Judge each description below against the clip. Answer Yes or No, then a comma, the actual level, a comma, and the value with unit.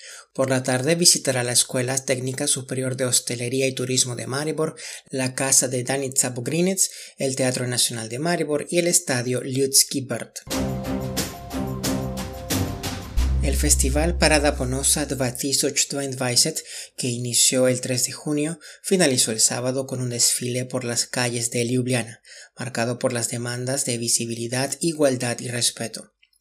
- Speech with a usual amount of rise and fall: No, narrow, 2.3 semitones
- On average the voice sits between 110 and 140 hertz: Yes, low, 130 Hz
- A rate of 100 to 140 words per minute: Yes, average, 135 wpm